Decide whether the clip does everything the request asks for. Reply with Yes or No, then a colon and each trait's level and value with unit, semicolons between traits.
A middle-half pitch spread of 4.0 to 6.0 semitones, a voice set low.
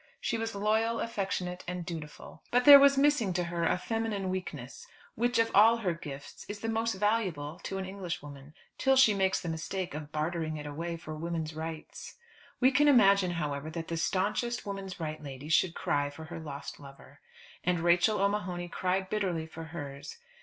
No: average, 4.8 semitones; medium, 180 Hz